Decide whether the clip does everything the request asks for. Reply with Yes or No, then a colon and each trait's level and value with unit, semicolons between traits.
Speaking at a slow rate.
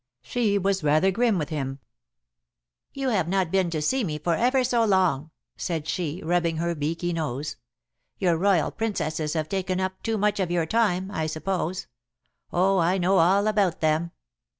No: average, 175 wpm